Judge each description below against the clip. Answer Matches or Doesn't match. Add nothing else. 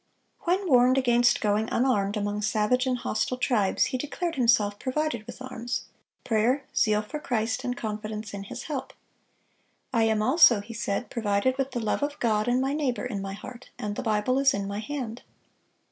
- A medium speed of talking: Matches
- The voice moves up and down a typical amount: Matches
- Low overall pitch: Doesn't match